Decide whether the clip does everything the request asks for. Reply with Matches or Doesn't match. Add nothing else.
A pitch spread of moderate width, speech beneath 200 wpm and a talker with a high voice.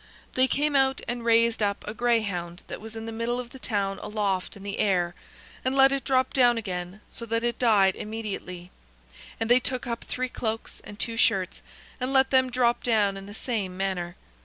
Doesn't match